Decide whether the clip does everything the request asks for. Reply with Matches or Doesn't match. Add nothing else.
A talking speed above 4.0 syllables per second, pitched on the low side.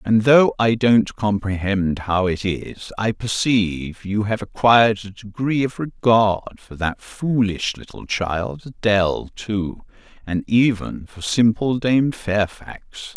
Doesn't match